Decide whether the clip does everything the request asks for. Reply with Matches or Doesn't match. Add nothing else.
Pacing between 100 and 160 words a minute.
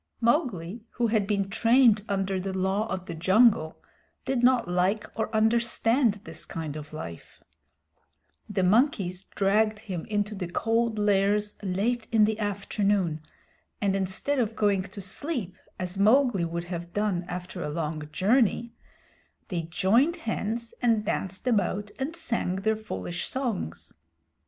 Matches